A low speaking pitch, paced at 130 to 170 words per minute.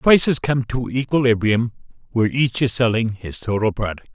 Yes: low, 120 Hz; average, 160 wpm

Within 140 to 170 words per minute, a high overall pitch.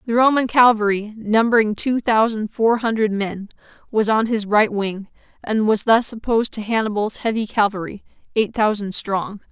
Yes: average, 160 wpm; high, 215 Hz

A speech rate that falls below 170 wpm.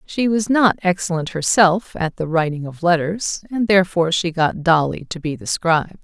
No: average, 190 wpm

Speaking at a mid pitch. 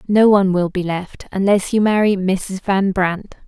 No: high, 195 Hz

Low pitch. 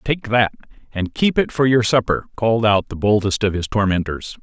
Yes: low, 110 Hz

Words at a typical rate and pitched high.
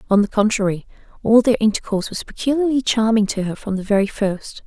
Yes: average, 195 wpm; high, 215 Hz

